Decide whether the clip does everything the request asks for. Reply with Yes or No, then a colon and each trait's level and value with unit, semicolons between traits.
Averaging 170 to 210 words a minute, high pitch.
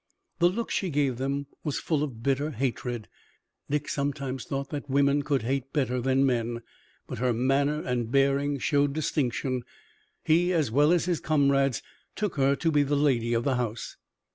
No: average, 175 wpm; medium, 140 Hz